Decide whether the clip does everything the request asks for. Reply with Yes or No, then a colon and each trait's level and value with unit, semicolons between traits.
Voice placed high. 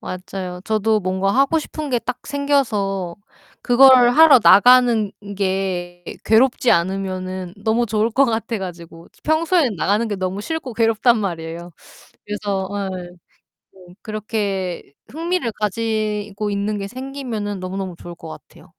Yes: high, 210 Hz